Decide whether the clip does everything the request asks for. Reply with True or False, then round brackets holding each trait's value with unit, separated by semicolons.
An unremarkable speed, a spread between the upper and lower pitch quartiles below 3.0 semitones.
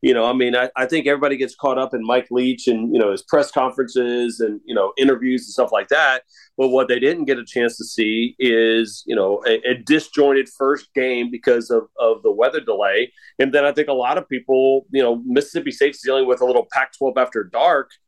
False (235 wpm; 2.5 semitones)